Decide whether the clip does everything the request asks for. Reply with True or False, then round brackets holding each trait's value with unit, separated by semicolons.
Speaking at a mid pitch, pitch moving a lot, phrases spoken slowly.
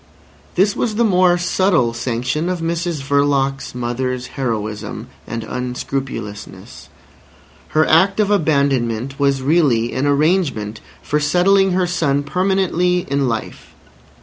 True (145 Hz; 6.0 semitones; 120 wpm)